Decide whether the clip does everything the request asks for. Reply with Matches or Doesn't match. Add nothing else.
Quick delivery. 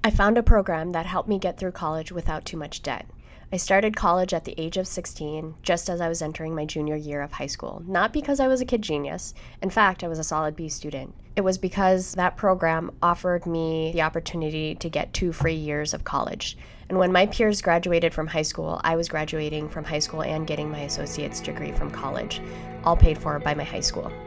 Matches